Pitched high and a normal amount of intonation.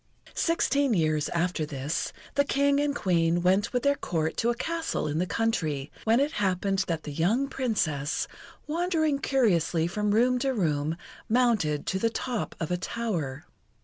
No: high, 200 Hz; wide, 7.8 semitones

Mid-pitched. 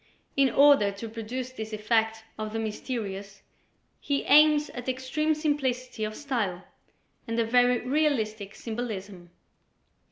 No: high, 230 Hz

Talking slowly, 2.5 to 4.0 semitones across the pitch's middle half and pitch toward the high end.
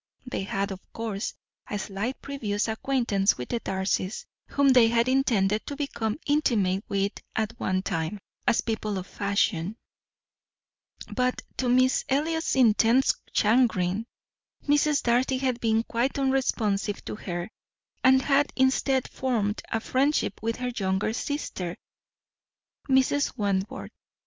No: slow, 130 wpm; average, 4.6 semitones; high, 230 Hz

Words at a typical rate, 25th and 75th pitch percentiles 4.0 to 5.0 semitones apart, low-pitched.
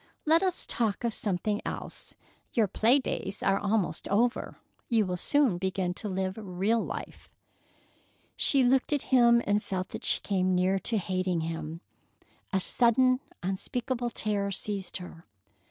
No: average, 150 wpm; average, 4.3 semitones; high, 205 Hz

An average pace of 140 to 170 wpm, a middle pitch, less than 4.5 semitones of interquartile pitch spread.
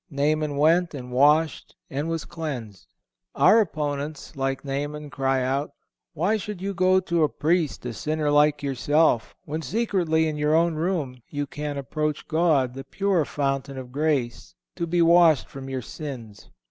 Yes: average, 160 wpm; medium, 150 Hz; average, 3.1 semitones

